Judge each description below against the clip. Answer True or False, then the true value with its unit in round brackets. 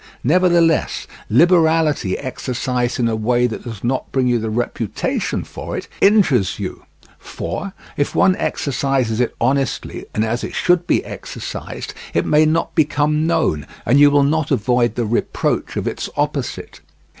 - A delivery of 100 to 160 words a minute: True (155 wpm)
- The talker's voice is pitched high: False (130 Hz)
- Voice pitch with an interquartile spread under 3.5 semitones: False (4.8 semitones)